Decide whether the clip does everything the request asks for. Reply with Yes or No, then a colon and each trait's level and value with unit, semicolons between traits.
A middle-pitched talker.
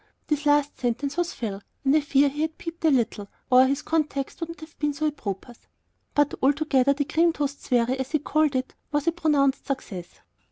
No: very high, 285 Hz